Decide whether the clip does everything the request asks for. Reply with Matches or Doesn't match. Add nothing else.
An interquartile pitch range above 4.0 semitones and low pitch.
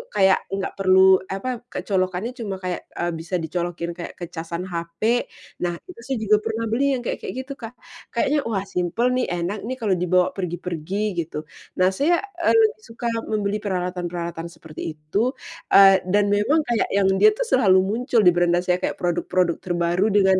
Doesn't match